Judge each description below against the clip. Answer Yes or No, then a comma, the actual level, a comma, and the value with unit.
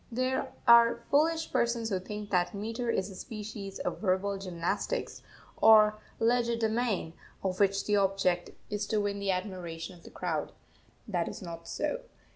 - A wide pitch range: No, average, 3.7 semitones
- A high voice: Yes, high, 205 Hz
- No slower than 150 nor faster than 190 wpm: Yes, average, 155 wpm